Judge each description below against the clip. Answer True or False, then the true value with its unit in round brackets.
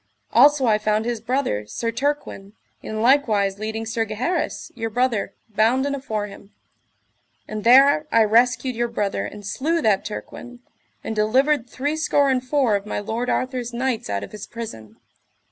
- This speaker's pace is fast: False (160 wpm)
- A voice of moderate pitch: False (230 Hz)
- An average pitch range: True (3.6 semitones)